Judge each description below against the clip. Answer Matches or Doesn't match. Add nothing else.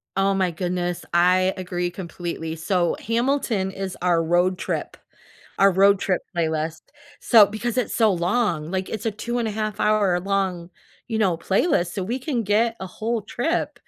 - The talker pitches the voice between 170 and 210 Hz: Matches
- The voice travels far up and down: Doesn't match